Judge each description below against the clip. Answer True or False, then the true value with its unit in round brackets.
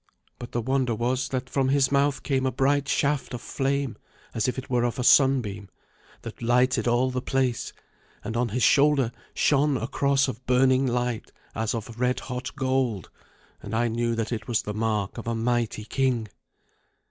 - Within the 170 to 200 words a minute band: True (180 wpm)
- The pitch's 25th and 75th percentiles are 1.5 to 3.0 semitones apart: True (2.4 semitones)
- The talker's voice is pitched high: False (125 Hz)